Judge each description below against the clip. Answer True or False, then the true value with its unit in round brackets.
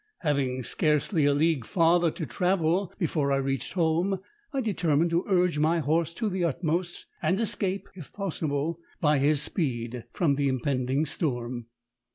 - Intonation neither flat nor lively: True (4.0 semitones)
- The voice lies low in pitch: False (160 Hz)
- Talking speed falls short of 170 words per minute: True (155 wpm)